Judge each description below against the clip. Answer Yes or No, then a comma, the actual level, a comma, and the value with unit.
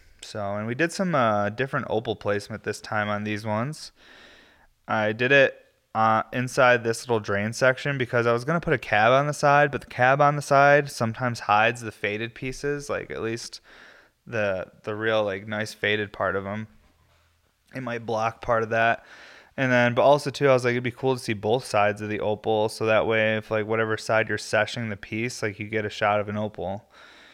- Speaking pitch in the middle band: No, low, 110 Hz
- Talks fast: Yes, fast, 220 wpm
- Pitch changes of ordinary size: Yes, average, 3.0 semitones